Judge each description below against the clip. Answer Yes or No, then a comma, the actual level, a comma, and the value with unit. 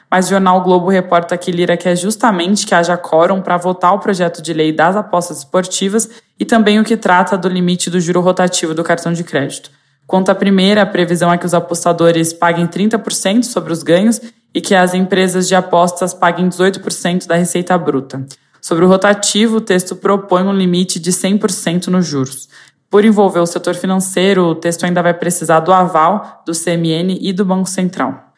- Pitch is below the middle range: No, medium, 180 Hz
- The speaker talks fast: Yes, fast, 195 wpm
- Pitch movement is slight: Yes, narrow, 1.9 semitones